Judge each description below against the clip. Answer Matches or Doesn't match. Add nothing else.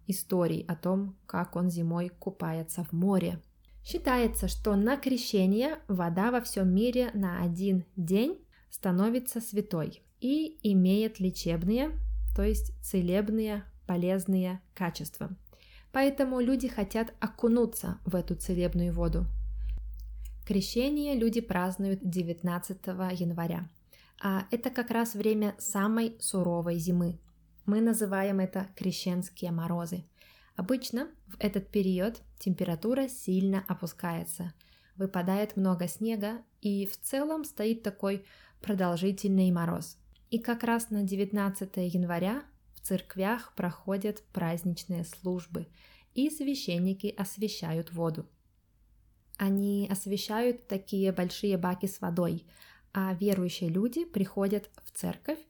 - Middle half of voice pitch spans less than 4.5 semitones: Matches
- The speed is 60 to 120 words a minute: Matches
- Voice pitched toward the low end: Doesn't match